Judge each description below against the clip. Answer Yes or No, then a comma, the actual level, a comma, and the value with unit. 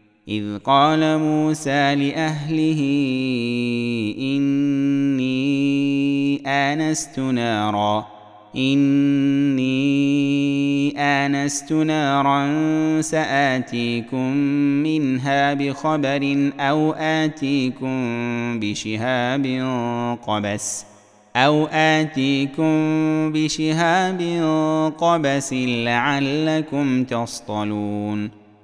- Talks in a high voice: No, medium, 140 Hz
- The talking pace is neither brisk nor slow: No, slow, 50 wpm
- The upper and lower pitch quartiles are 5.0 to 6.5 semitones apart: No, average, 3.9 semitones